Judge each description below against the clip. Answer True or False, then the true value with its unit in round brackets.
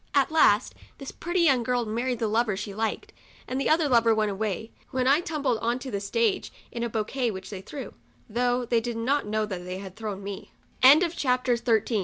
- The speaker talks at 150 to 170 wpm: False (195 wpm)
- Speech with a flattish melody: False (3.6 semitones)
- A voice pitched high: True (235 Hz)